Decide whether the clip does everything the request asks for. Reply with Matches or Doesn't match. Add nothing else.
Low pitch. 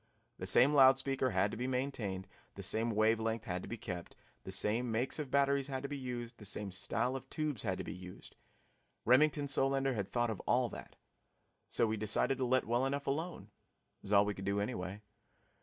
Matches